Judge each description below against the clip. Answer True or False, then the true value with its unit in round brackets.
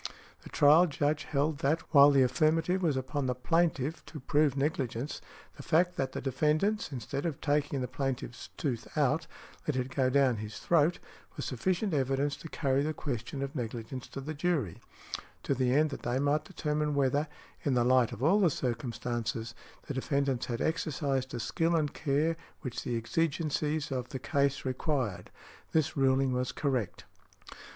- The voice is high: False (140 Hz)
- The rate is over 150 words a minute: True (170 wpm)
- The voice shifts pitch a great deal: False (3.2 semitones)